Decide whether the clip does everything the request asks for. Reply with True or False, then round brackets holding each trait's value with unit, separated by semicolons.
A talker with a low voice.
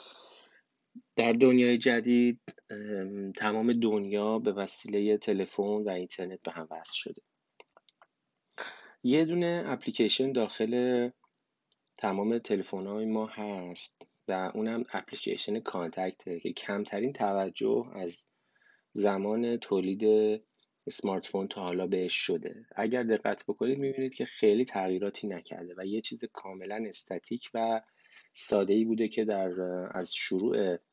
True (105 Hz)